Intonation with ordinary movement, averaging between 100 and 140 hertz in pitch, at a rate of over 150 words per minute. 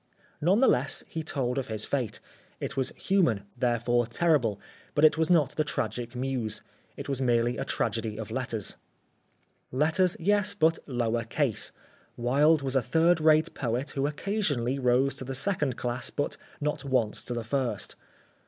Yes: average, 4.4 semitones; low, 135 Hz; average, 165 wpm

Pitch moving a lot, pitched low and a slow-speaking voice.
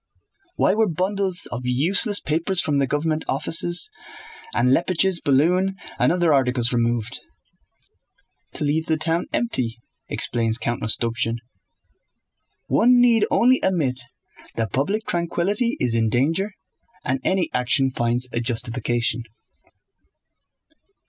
No: wide, 7.2 semitones; medium, 150 Hz; slow, 115 wpm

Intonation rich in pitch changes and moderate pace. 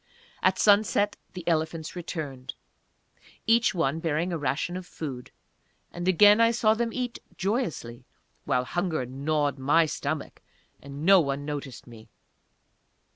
No: wide, 5.8 semitones; slow, 130 wpm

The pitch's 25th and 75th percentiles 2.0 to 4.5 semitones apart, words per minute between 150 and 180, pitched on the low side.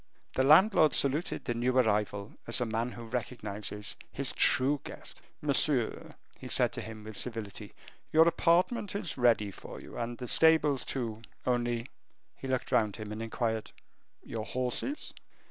Yes: average, 3.9 semitones; average, 160 wpm; low, 120 Hz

